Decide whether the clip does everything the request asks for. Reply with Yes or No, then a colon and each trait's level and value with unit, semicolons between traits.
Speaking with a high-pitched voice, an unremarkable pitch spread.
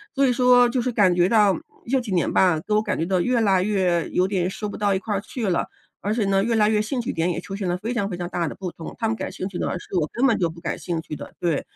Yes: high, 195 Hz; average, 3.9 semitones